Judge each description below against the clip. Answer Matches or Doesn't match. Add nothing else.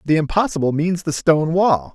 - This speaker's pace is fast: Doesn't match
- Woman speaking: Doesn't match